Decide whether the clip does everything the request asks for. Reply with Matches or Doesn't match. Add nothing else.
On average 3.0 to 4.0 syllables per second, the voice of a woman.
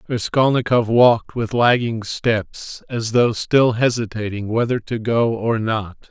Doesn't match